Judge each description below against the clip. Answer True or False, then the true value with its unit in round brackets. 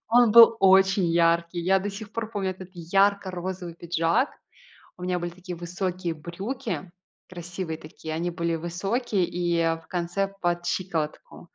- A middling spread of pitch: False (2.3 semitones)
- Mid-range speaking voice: True (180 Hz)